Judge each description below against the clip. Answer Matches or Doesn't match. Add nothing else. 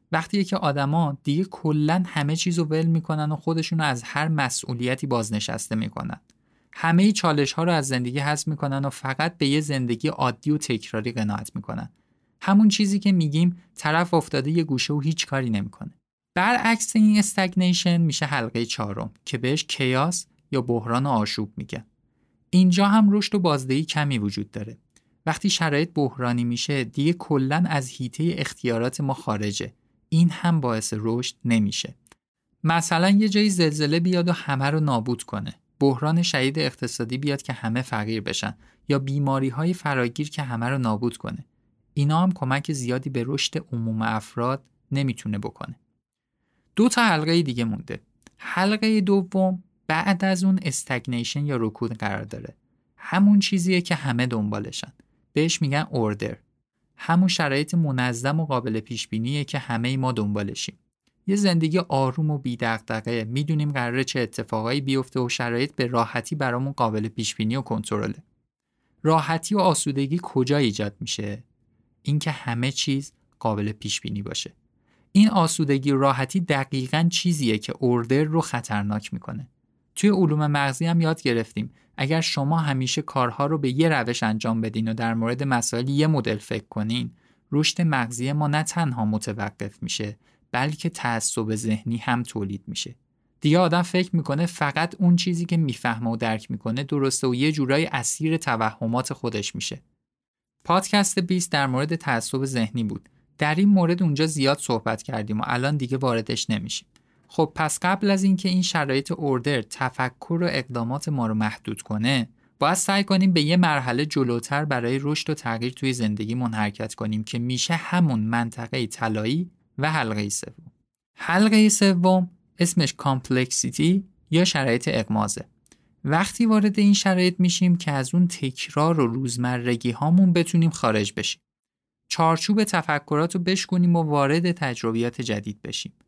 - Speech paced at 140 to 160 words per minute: Matches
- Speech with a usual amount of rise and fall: Doesn't match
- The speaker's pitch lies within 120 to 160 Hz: Matches